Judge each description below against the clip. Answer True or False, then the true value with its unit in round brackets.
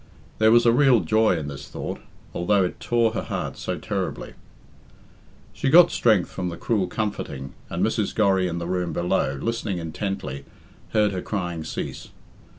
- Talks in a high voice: False (95 Hz)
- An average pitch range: True (4.5 semitones)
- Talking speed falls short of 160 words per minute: False (165 wpm)